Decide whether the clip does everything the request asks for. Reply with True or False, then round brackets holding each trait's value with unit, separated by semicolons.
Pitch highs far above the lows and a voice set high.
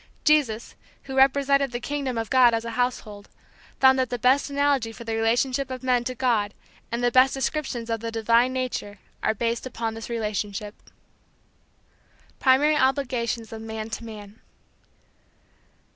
False (2.7 semitones; 240 Hz)